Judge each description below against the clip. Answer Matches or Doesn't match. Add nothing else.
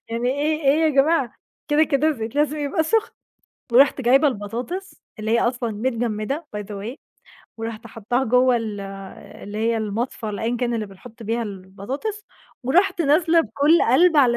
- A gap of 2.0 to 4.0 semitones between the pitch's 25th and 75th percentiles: Doesn't match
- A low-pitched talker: Doesn't match